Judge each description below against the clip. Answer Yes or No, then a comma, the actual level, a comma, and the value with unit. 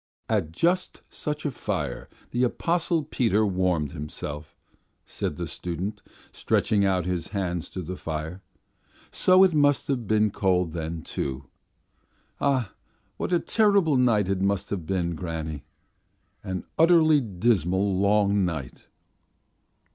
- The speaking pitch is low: Yes, low, 100 Hz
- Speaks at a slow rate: Yes, slow, 130 wpm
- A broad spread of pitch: Yes, wide, 6.8 semitones